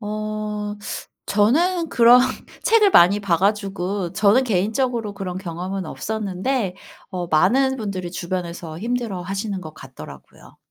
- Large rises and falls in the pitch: No, average, 3.9 semitones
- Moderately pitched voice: No, high, 200 Hz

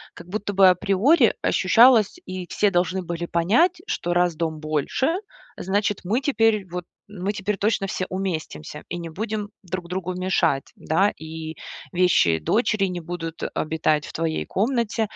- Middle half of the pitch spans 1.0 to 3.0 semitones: No, average, 3.7 semitones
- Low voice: No, medium, 185 Hz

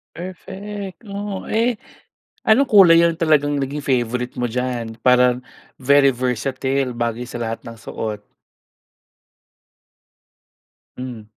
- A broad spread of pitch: Yes, wide, 5.9 semitones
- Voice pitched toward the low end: Yes, low, 130 Hz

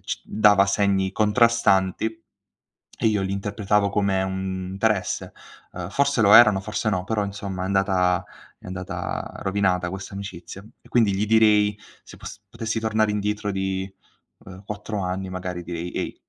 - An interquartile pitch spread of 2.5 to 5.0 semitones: No, narrow, 1.9 semitones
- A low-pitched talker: Yes, low, 100 Hz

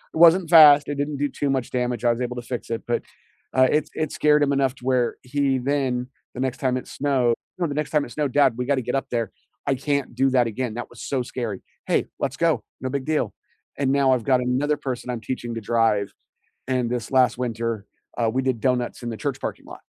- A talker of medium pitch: No, low, 130 Hz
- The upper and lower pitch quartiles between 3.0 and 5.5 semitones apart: No, narrow, 2.6 semitones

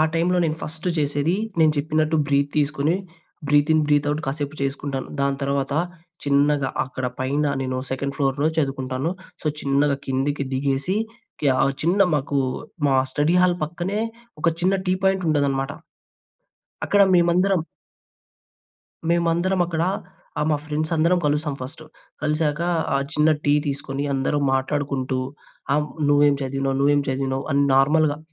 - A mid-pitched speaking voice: Yes, medium, 145 Hz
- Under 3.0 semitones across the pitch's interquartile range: Yes, narrow, 2.4 semitones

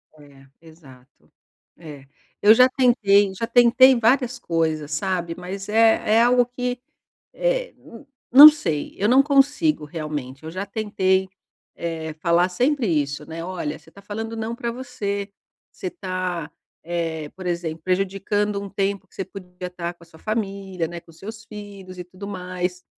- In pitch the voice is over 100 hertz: Yes, high, 190 Hz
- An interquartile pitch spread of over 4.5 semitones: Yes, average, 4.9 semitones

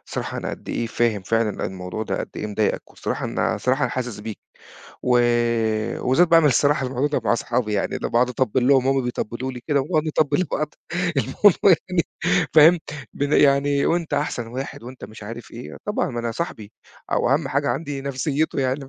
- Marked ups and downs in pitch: No, average, 3.8 semitones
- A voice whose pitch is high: No, low, 130 Hz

